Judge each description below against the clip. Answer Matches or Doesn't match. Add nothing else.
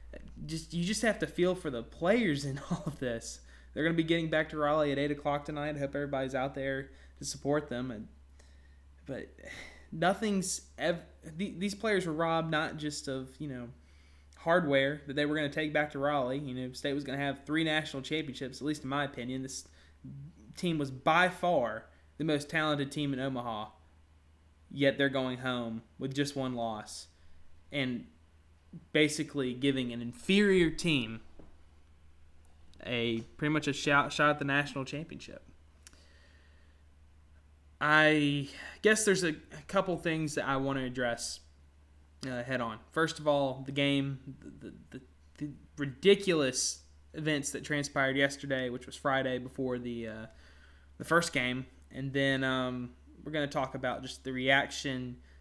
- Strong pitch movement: Matches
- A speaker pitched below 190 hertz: Matches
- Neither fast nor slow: Matches